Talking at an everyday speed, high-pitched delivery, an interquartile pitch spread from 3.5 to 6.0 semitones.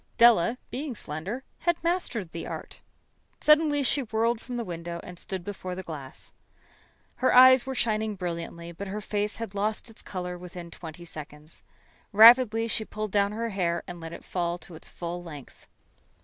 Yes: average, 175 wpm; high, 200 Hz; average, 5.3 semitones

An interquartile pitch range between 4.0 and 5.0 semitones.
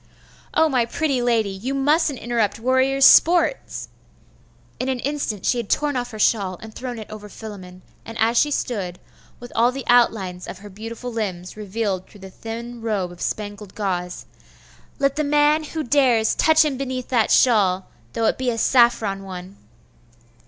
Yes: average, 4.4 semitones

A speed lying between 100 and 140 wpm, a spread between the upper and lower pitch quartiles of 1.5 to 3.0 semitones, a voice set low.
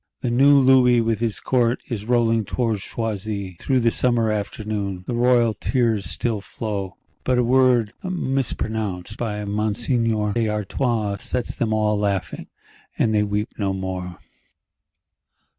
Yes: slow, 135 wpm; average, 2.7 semitones; low, 110 Hz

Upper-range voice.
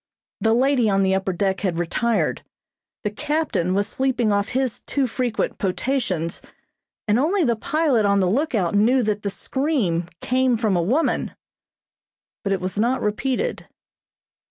Yes: high, 220 Hz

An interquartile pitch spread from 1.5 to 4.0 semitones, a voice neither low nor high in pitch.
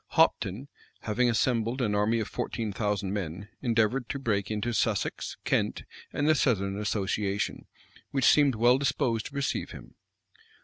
No: average, 3.5 semitones; low, 115 Hz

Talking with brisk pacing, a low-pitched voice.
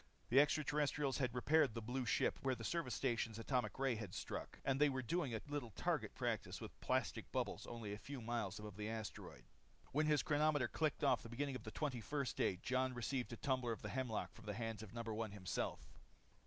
Yes: fast, 220 wpm; low, 125 Hz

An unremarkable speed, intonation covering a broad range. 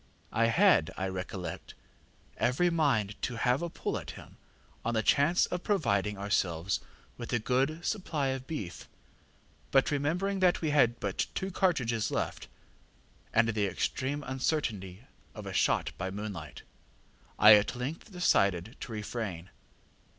Yes: average, 145 wpm; wide, 6.8 semitones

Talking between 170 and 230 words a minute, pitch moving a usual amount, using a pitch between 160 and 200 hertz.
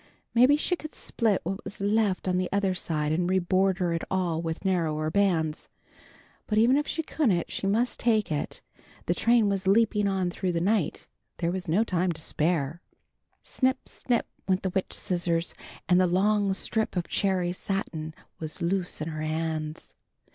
Yes: average, 175 wpm; average, 3.5 semitones; medium, 185 Hz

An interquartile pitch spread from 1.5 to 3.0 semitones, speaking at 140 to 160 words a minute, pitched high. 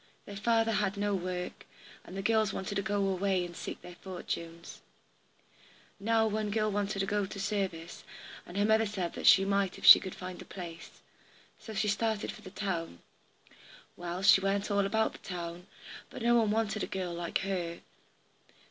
No: average, 2.7 semitones; average, 185 wpm; high, 195 Hz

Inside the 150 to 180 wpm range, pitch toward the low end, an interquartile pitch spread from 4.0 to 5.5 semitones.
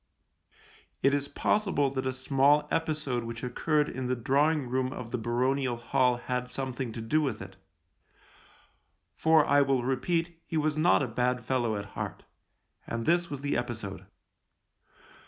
No: average, 160 wpm; low, 130 Hz; average, 3.3 semitones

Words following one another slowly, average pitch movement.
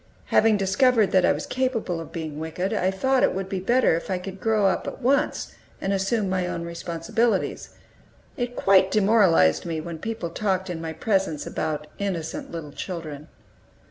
No: average, 175 wpm; average, 4.5 semitones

